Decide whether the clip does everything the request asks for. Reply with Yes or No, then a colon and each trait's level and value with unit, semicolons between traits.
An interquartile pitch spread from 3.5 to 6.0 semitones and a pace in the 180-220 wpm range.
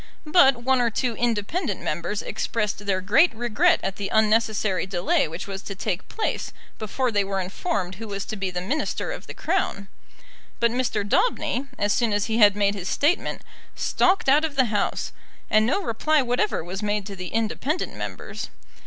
Yes: average, 4.4 semitones; average, 185 wpm